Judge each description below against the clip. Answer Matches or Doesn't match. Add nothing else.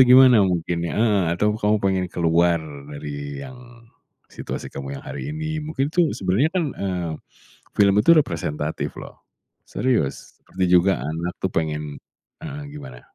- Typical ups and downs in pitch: Doesn't match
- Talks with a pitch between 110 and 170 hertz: Doesn't match